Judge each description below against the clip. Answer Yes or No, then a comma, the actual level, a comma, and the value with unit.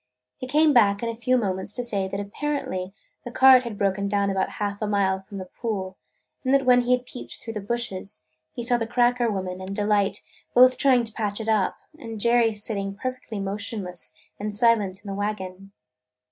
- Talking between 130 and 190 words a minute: No, average, 200 wpm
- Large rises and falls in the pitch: No, average, 3.5 semitones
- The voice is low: No, high, 210 Hz